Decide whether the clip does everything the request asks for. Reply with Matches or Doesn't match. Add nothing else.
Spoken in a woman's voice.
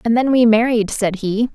Matches